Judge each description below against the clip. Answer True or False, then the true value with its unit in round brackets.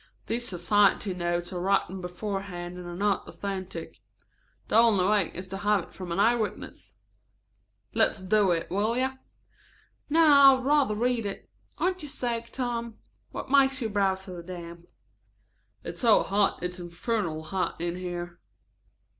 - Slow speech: False (155 wpm)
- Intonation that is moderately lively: True (4.7 semitones)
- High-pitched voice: True (200 Hz)